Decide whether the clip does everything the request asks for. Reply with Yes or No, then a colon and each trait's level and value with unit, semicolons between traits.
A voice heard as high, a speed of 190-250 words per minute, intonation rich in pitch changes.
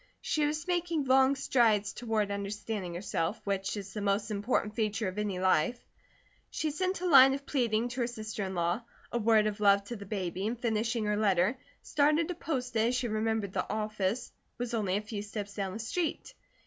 No: high, 215 Hz; average, 200 wpm; average, 3.6 semitones